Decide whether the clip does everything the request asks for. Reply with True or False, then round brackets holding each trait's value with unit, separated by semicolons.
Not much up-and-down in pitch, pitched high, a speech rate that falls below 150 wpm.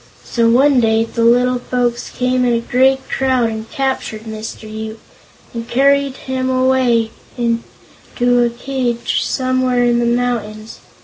True (1.9 semitones; 245 Hz; 140 wpm)